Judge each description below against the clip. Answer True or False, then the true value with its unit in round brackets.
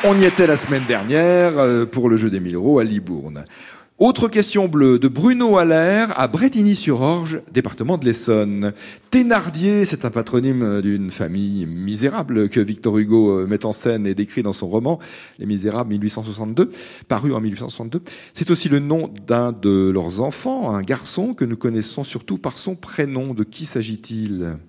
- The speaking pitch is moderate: False (120 Hz)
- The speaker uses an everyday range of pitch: False (7.7 semitones)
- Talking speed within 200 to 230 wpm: False (170 wpm)